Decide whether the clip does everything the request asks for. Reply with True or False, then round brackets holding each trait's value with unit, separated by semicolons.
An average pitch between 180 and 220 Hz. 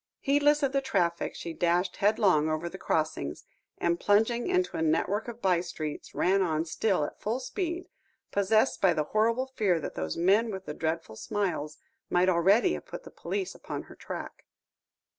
True (190 Hz)